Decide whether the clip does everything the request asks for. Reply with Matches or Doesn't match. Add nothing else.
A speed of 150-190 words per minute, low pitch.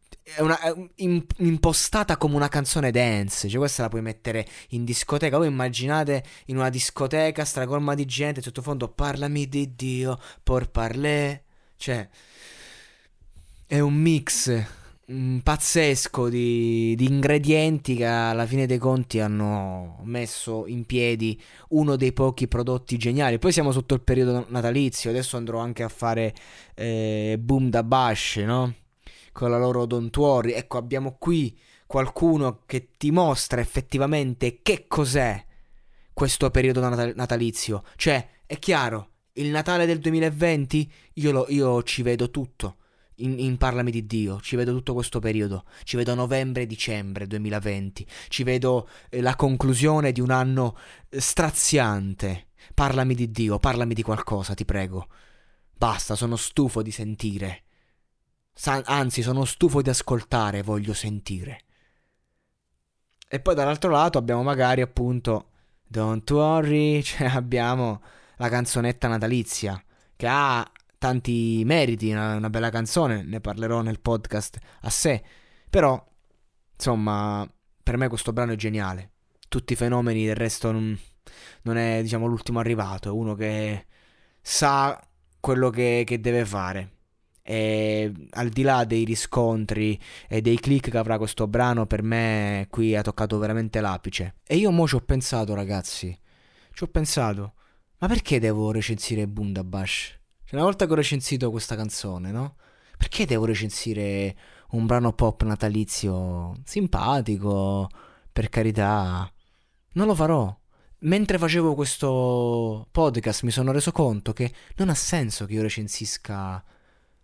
Doesn't match